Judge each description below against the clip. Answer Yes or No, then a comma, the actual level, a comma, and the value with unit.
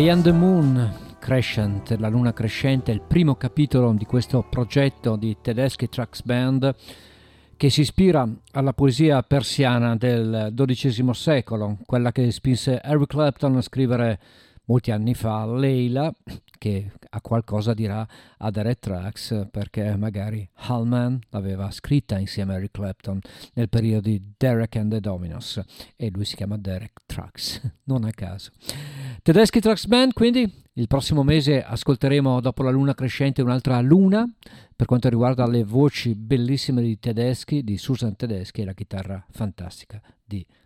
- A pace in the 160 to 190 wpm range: No, average, 150 wpm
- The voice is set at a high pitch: No, low, 120 Hz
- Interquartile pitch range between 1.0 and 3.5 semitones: No, average, 3.9 semitones